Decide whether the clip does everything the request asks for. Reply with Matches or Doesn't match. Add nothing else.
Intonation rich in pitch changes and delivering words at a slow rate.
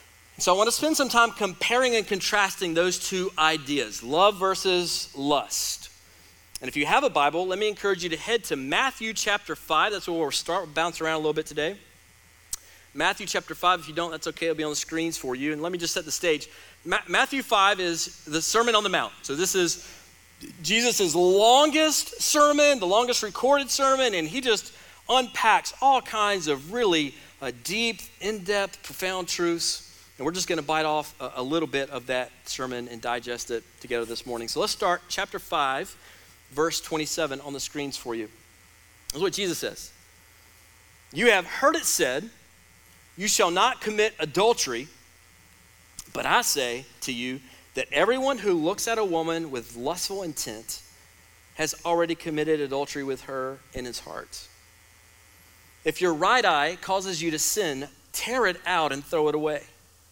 Doesn't match